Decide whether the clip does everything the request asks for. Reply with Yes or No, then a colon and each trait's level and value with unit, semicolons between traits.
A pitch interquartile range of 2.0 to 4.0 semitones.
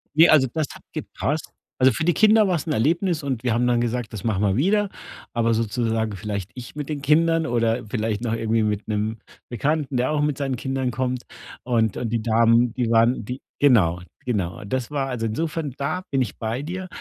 No: average, 4.6 semitones